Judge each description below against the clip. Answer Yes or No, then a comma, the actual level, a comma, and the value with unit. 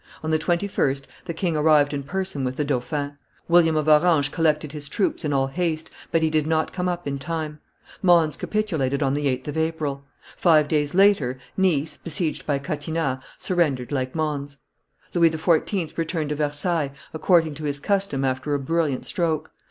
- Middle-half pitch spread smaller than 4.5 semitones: Yes, average, 2.7 semitones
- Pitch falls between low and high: Yes, medium, 155 Hz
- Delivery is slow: No, average, 175 wpm